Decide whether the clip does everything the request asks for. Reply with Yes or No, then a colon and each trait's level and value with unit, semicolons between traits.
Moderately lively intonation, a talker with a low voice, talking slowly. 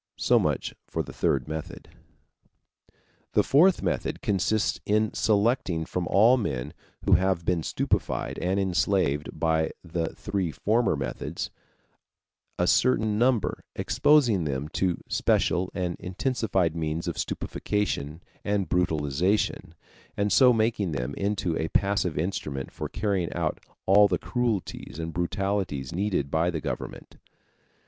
Yes: average, 4.3 semitones; very low, 90 Hz; slow, 130 wpm